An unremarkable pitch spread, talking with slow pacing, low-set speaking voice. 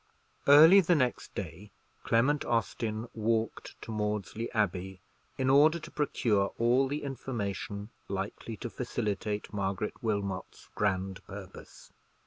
Yes: average, 4.2 semitones; slow, 115 wpm; low, 110 Hz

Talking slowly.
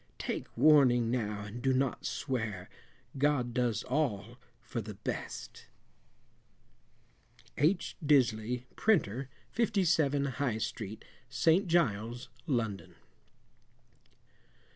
Yes: slow, 90 wpm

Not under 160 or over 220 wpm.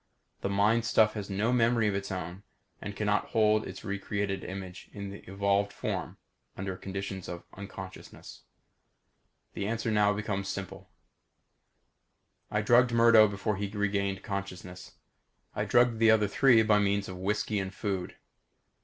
No: average, 145 wpm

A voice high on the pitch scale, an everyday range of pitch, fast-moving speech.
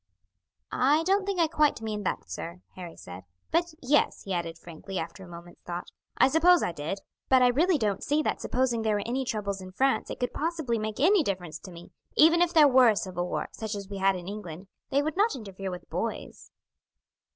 No: high, 215 Hz; wide, 8.2 semitones; fast, 220 wpm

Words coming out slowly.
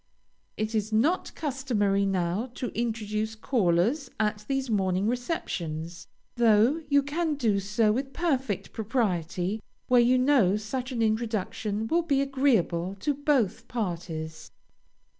Yes: slow, 125 wpm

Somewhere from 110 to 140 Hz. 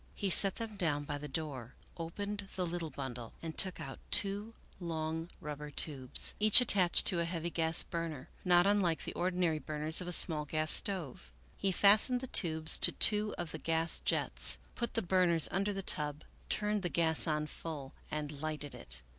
No: medium, 165 Hz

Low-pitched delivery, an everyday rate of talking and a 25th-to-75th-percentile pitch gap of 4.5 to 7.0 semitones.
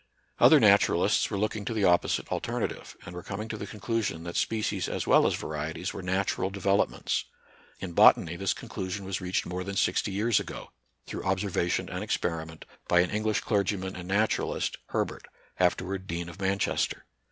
No: very low, 95 Hz; average, 170 wpm; narrow, 2.4 semitones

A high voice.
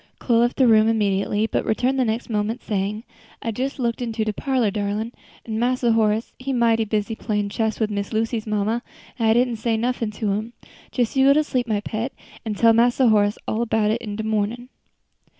Yes: high, 225 Hz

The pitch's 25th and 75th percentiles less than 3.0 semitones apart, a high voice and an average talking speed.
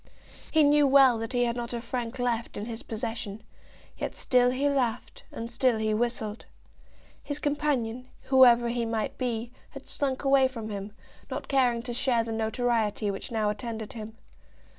Yes: narrow, 2.5 semitones; high, 235 Hz; average, 170 wpm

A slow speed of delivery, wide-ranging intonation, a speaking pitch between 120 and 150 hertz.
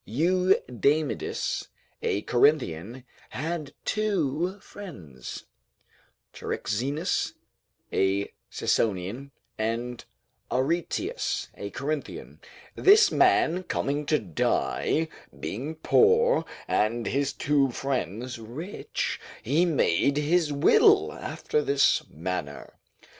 Yes: slow, 85 wpm; wide, 6.2 semitones; medium, 140 Hz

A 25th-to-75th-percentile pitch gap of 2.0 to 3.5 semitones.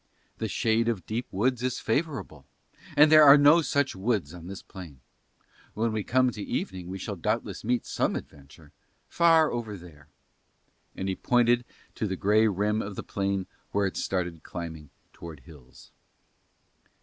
No: wide, 5.5 semitones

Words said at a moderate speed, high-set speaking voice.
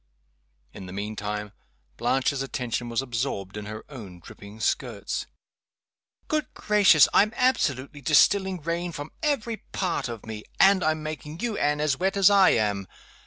No: average, 155 wpm; medium, 145 Hz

